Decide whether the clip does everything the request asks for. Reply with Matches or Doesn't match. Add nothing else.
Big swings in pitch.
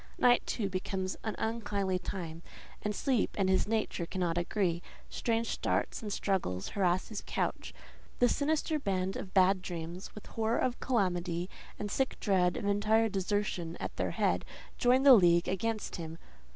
Doesn't match